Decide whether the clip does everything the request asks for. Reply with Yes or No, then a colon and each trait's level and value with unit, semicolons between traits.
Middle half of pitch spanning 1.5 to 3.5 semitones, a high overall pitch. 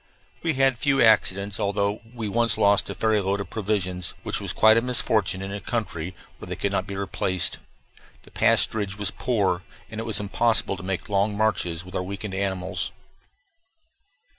No: narrow, 2.4 semitones; low, 100 Hz